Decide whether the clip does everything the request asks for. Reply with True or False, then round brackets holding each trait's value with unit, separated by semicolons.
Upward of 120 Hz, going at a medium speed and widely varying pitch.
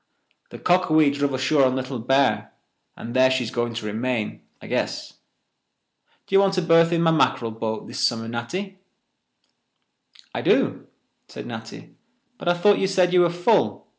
True (140 Hz; 165 wpm; 6.8 semitones)